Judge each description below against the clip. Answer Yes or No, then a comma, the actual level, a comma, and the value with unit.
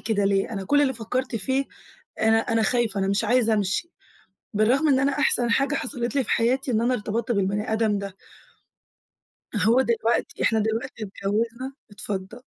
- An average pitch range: Yes, average, 3.4 semitones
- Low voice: No, high, 230 Hz